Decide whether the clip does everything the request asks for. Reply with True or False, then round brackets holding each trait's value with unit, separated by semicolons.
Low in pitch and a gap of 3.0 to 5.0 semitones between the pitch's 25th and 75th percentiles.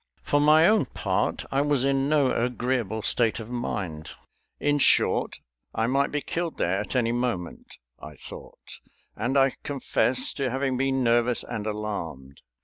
True (125 Hz; 4.5 semitones)